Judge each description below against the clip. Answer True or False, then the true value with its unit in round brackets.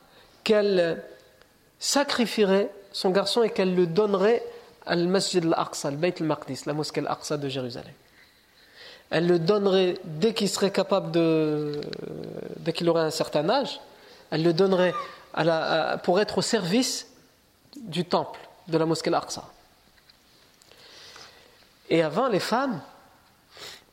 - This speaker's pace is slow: True (130 wpm)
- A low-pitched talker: False (190 Hz)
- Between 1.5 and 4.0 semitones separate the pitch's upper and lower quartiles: False (4.8 semitones)